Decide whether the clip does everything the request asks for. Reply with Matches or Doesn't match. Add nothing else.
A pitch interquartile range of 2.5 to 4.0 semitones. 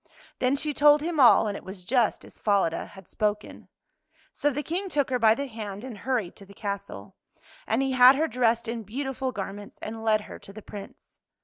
Doesn't match